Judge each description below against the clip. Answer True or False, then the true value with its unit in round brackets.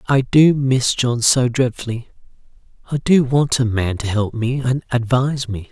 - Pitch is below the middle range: True (125 Hz)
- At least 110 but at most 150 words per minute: False (180 wpm)